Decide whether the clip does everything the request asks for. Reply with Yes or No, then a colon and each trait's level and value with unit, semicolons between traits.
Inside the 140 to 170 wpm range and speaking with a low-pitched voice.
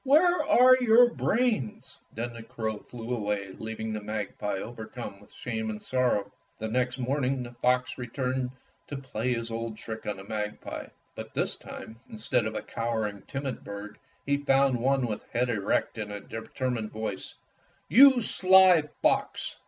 Yes: average, 165 wpm; low, 120 Hz